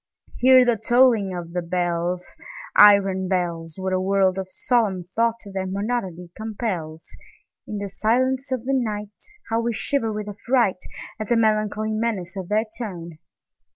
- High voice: Yes, high, 205 Hz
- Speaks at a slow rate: Yes, slow, 130 wpm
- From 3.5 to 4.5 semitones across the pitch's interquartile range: Yes, average, 3.9 semitones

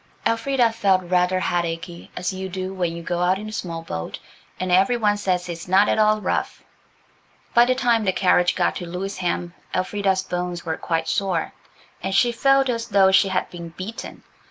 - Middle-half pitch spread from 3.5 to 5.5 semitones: No, average, 3.0 semitones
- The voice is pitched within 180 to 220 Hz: Yes, medium, 185 Hz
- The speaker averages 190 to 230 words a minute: Yes, average, 195 wpm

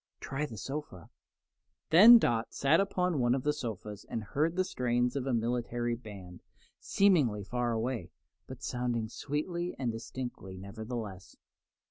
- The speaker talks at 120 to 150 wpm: Yes, average, 140 wpm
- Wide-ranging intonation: No, average, 4.9 semitones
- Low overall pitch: Yes, low, 120 Hz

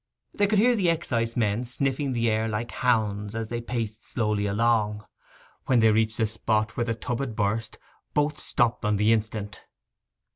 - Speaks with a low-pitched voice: Yes, low, 115 Hz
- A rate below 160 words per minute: No, average, 175 wpm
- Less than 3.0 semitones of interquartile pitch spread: Yes, narrow, 2.5 semitones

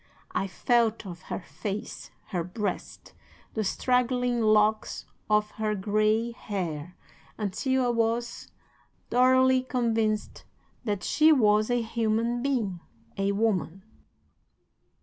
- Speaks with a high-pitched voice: Yes, high, 220 Hz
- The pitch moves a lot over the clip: No, average, 3.0 semitones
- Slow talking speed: Yes, slow, 110 wpm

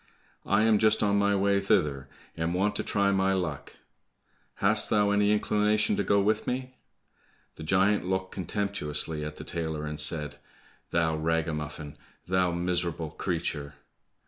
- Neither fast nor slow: Yes, average, 145 wpm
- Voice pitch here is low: Yes, very low, 95 Hz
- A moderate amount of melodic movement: Yes, average, 4.4 semitones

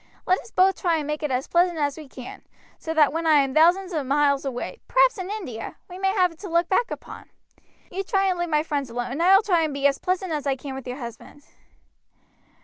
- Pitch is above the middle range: Yes, very high, 320 Hz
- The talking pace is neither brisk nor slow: No, fast, 250 wpm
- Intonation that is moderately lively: Yes, average, 4.8 semitones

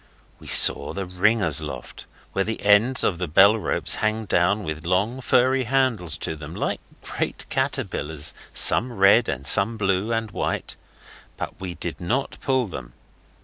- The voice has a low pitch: Yes, low, 100 Hz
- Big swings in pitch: No, average, 4.7 semitones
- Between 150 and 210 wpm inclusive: Yes, average, 155 wpm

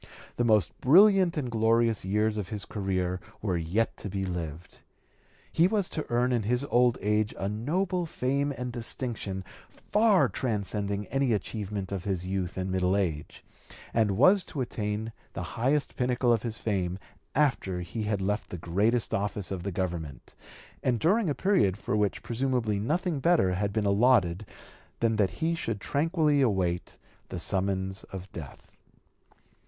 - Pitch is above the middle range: No, low, 110 Hz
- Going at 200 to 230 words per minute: No, average, 165 wpm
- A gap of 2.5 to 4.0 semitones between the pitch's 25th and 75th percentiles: No, average, 5.1 semitones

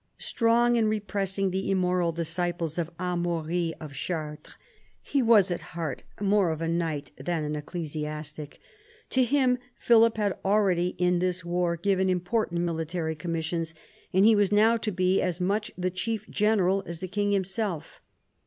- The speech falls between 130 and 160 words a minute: Yes, average, 155 wpm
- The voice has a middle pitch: Yes, medium, 180 Hz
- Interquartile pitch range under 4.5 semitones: Yes, average, 3.6 semitones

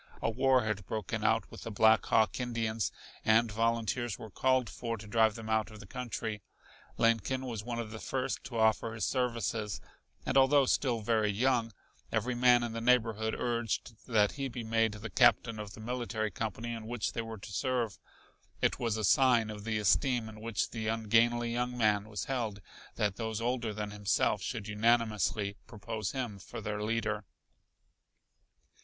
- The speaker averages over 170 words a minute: Yes, average, 180 wpm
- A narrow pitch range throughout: Yes, narrow, 1.9 semitones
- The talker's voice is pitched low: Yes, low, 115 Hz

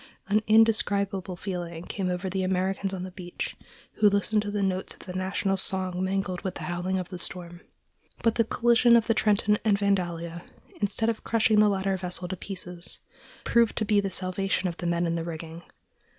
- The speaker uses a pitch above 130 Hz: Yes, high, 190 Hz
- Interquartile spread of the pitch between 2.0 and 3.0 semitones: Yes, narrow, 2.5 semitones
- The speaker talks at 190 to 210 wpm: Yes, average, 195 wpm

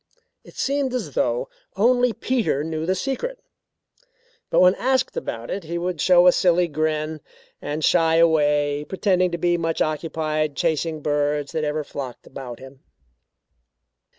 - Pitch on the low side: No, medium, 160 Hz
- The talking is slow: No, average, 150 wpm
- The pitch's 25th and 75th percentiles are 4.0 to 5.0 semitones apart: No, average, 3.5 semitones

